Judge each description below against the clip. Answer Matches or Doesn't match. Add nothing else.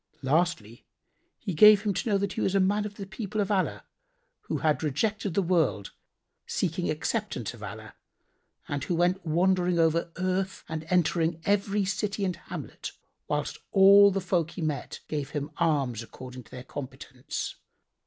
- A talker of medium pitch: Matches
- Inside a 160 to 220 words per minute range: Matches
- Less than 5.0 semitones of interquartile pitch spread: Matches